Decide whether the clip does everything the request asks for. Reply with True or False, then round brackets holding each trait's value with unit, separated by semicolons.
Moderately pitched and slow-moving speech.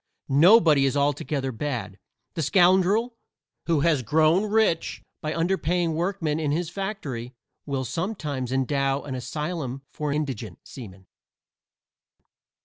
True (150 Hz; 115 wpm)